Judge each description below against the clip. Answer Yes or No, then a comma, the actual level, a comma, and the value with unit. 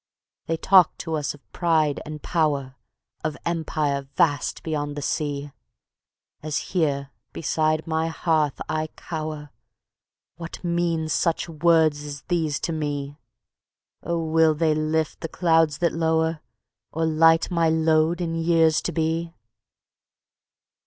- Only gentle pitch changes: Yes, narrow, 1.6 semitones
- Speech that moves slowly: Yes, slow, 130 wpm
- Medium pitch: Yes, medium, 160 Hz